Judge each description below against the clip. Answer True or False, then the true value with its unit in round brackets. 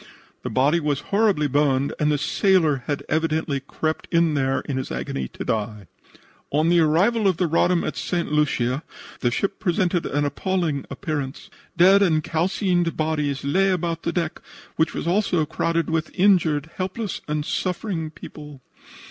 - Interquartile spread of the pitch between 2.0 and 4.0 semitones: True (3.6 semitones)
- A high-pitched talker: False (160 Hz)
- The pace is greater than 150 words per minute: True (160 wpm)